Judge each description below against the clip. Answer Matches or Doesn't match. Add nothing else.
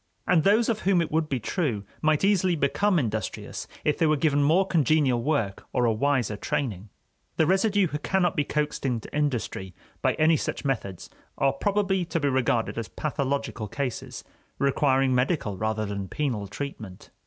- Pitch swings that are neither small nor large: Doesn't match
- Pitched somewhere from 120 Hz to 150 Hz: Matches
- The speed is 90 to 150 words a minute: Doesn't match